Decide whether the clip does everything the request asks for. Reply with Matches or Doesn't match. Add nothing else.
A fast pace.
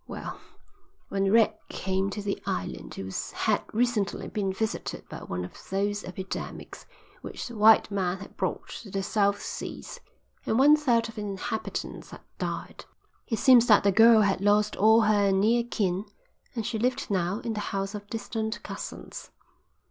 Doesn't match